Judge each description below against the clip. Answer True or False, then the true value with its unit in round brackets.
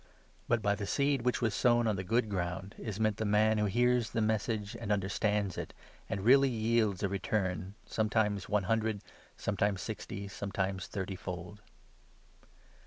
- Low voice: True (105 Hz)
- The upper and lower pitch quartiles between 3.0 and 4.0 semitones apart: False (2.4 semitones)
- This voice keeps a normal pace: True (175 wpm)